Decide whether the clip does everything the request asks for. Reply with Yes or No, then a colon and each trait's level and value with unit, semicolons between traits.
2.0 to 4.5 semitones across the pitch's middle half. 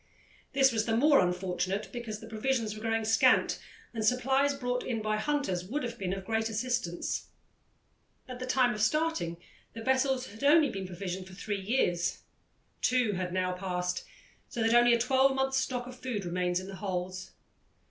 No: average, 5.2 semitones